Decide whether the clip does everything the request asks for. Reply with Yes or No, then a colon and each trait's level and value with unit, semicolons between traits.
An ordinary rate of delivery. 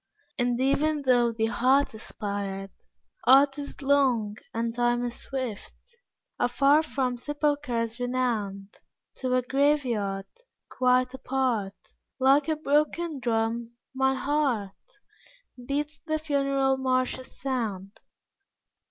No: slow, 105 wpm